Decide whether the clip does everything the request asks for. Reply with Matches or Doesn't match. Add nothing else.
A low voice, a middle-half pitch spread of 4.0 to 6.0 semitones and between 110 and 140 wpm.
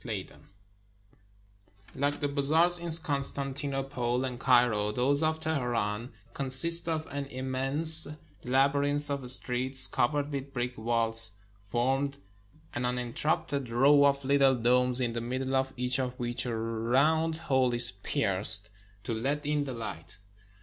Doesn't match